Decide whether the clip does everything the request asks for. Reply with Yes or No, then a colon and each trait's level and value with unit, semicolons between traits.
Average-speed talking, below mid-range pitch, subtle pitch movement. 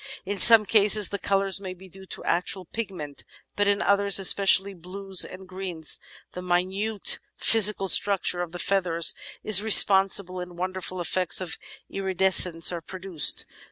No: average, 150 wpm; high, 190 Hz; narrow, 1.8 semitones